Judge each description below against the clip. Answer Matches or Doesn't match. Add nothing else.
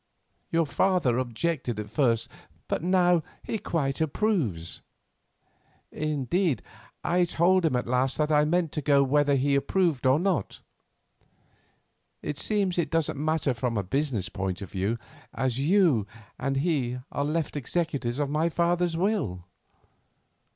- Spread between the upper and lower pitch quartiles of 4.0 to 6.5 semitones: Matches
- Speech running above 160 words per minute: Doesn't match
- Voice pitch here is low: Doesn't match